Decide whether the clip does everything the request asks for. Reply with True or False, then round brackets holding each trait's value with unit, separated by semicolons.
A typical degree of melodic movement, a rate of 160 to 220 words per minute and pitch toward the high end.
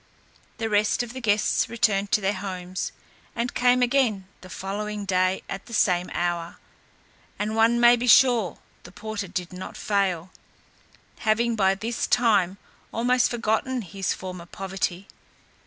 False (3.8 semitones; 145 wpm; 205 Hz)